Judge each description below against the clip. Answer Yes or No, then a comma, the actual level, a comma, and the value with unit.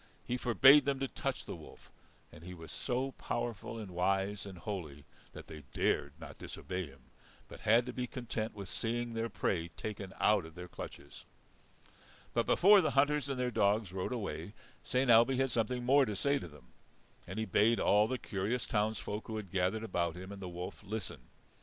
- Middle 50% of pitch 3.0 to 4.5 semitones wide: No, average, 4.9 semitones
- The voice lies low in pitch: Yes, low, 110 Hz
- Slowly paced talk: No, average, 195 wpm